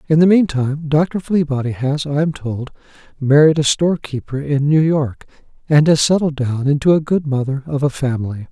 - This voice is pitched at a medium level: Yes, medium, 145 Hz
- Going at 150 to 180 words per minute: No, average, 190 wpm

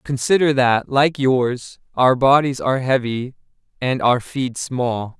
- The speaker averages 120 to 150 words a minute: Yes, average, 140 wpm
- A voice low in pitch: Yes, low, 130 Hz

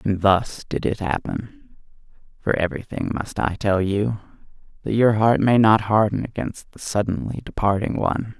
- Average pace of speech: Yes, average, 150 wpm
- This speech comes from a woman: No, male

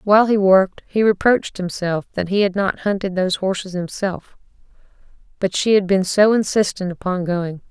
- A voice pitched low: No, high, 190 Hz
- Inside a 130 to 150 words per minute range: No, average, 170 wpm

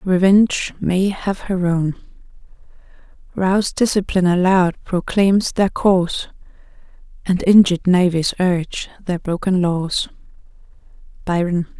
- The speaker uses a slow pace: Yes, slow, 95 wpm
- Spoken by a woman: Yes, female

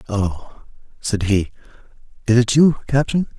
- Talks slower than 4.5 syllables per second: Yes, 4.1 syllables/s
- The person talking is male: Yes, male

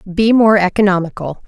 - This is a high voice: Yes, high, 195 Hz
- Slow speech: Yes, slow, 120 wpm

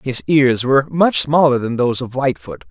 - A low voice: Yes, low, 130 Hz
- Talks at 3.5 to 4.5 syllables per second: No, 5.4 syllables/s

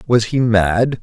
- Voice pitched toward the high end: No, low, 115 Hz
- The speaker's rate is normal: Yes, average, 175 wpm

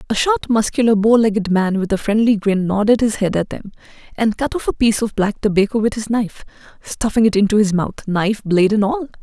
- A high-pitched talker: Yes, high, 215 Hz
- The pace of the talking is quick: Yes, fast, 220 wpm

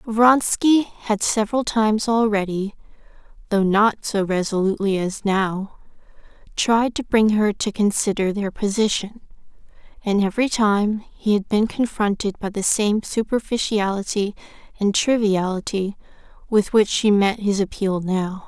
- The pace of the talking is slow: Yes, slow, 125 wpm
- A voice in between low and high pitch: No, high, 210 Hz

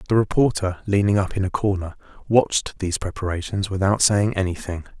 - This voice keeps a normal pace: Yes, average, 155 wpm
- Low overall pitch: Yes, low, 100 Hz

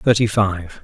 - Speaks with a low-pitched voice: Yes, low, 100 Hz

